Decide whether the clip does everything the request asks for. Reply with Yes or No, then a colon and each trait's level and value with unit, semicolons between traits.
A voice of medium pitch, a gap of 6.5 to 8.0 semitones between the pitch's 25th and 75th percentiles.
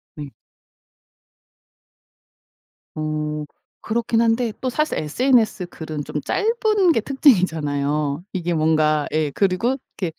Yes: medium, 175 Hz; wide, 7.7 semitones